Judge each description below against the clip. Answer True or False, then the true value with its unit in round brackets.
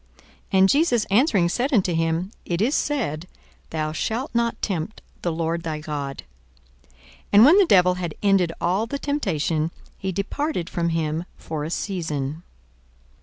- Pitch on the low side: False (180 Hz)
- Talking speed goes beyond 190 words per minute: False (160 wpm)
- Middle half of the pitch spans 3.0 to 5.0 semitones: False (5.5 semitones)